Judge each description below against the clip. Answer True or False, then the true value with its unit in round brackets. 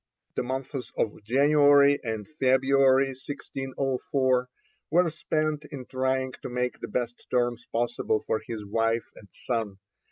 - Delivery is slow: True (130 wpm)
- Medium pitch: False (130 Hz)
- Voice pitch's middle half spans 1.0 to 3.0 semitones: True (2.5 semitones)